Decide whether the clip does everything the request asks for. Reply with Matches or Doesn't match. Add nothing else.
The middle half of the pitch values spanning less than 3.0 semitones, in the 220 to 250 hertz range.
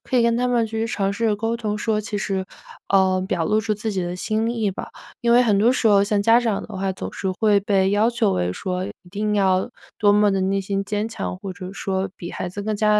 Doesn't match